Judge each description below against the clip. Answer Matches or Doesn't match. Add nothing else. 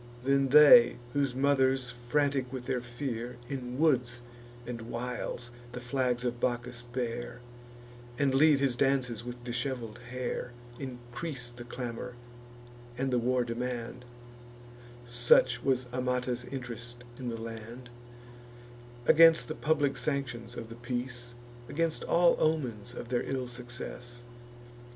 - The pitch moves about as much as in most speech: Doesn't match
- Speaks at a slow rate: Matches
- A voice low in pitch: Matches